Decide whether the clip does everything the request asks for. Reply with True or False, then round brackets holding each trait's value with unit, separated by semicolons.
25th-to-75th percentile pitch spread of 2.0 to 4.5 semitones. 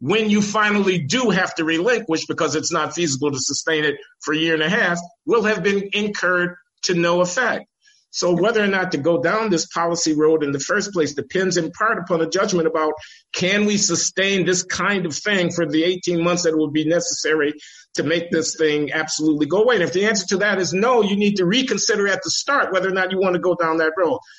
True (3.8 semitones)